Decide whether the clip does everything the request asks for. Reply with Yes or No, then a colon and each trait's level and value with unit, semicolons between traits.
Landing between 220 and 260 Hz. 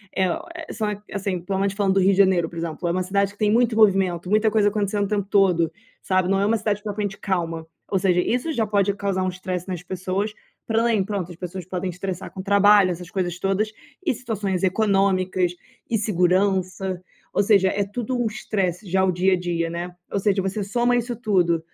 No: high, 195 Hz